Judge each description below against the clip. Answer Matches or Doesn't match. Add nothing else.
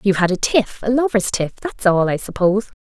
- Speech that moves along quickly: Doesn't match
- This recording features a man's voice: Doesn't match